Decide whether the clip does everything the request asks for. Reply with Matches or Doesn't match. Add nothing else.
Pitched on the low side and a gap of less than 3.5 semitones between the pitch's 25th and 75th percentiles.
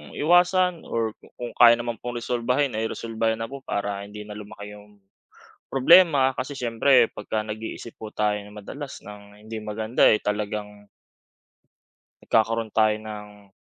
Matches